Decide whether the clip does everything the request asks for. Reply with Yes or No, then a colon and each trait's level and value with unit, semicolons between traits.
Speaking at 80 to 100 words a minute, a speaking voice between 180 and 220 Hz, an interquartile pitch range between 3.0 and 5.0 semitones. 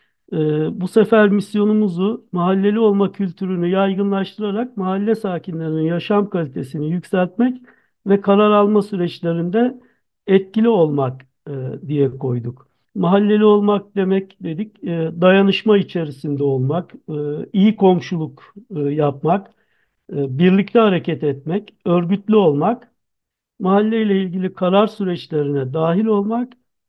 Yes: slow, 95 wpm; high, 190 Hz; average, 4.3 semitones